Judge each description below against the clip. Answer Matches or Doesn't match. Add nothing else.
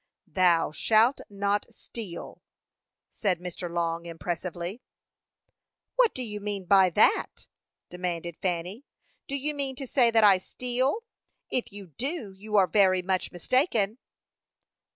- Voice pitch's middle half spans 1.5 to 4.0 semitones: Doesn't match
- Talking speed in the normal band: Doesn't match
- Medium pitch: Doesn't match